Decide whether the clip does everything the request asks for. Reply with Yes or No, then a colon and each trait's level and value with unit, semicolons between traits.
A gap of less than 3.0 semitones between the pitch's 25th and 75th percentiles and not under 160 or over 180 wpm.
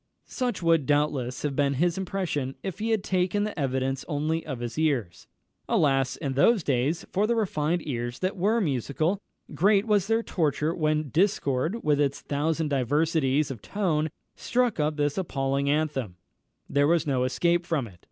No: average, 4.9 semitones; average, 170 wpm